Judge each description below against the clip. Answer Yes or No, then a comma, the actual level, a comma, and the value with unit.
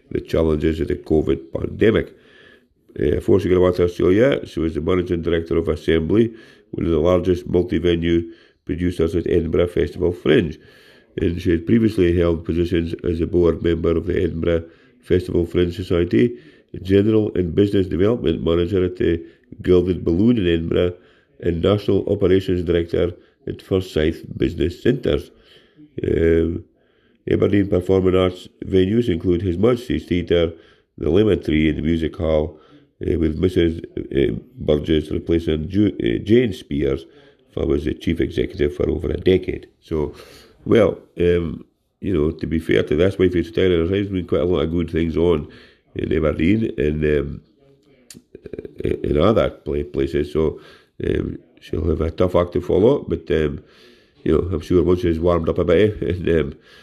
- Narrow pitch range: Yes, narrow, 2.1 semitones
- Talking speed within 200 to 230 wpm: No, average, 160 wpm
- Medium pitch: No, very low, 85 Hz